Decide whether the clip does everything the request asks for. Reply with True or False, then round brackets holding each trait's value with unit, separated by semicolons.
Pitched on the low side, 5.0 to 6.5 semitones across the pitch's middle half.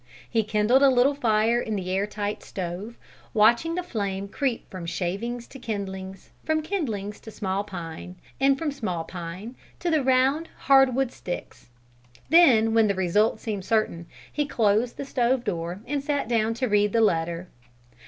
False (220 Hz; 5.3 semitones)